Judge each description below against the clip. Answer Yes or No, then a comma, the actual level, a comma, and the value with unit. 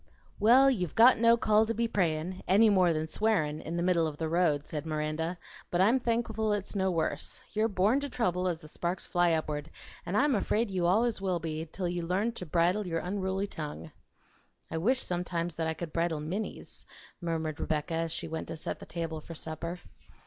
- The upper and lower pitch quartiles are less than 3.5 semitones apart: No, average, 4.4 semitones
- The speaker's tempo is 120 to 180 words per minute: No, fast, 205 wpm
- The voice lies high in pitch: No, medium, 175 Hz